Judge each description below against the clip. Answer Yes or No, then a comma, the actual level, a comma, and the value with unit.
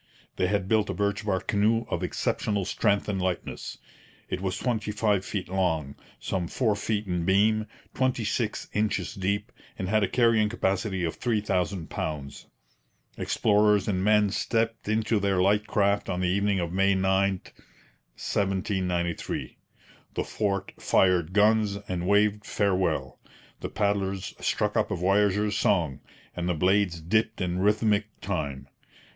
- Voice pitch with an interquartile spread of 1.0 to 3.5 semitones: Yes, narrow, 2.4 semitones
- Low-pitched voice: Yes, low, 100 Hz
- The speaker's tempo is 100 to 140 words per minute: No, average, 150 wpm